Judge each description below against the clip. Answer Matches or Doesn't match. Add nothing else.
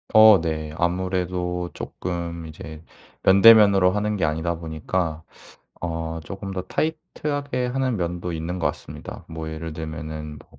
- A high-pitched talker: Doesn't match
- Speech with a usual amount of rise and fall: Matches